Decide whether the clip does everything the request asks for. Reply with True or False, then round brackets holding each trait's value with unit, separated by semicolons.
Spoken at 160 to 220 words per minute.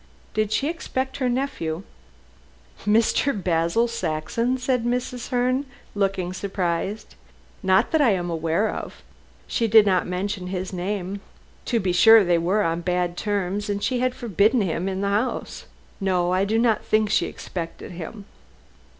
False (150 wpm)